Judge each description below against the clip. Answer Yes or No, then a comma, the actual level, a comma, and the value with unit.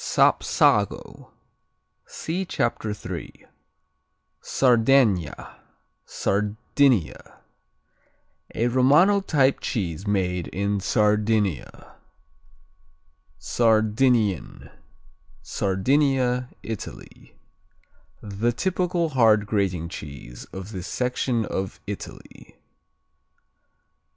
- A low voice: Yes, low, 110 Hz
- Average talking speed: No, slow, 60 wpm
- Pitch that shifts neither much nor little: Yes, average, 4.9 semitones